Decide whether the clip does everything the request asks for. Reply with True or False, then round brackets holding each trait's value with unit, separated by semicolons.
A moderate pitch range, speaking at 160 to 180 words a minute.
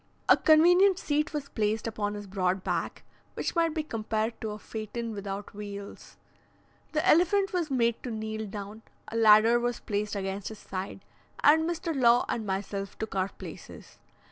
False (6.4 semitones; 170 wpm)